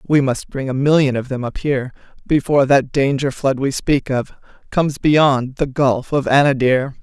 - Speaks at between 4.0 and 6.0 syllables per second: Yes, 4.8 syllables/s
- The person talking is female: Yes, female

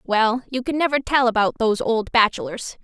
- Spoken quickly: No, average, 190 wpm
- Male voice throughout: No, female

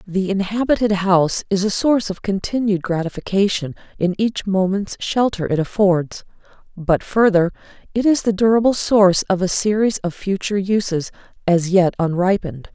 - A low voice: No, high, 195 Hz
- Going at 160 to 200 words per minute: No, average, 145 wpm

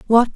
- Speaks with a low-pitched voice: No, high, 235 Hz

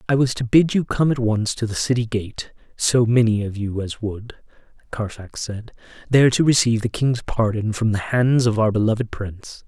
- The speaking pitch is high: No, low, 115 Hz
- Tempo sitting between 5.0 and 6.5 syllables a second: Yes, 5.1 syllables/s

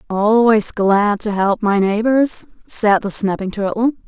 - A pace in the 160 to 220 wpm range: No, average, 145 wpm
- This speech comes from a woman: Yes, female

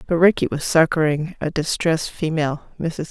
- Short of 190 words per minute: Yes, slow, 135 wpm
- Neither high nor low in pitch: Yes, medium, 160 Hz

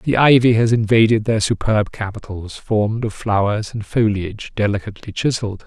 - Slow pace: No, average, 150 wpm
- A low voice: Yes, low, 110 Hz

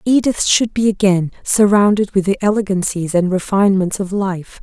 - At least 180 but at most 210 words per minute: No, average, 155 wpm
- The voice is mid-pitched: No, high, 195 Hz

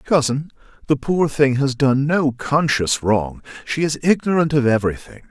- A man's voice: Yes, male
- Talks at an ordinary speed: Yes, average, 160 wpm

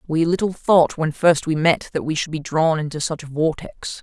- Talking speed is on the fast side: Yes, fast, 240 wpm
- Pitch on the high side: No, medium, 160 Hz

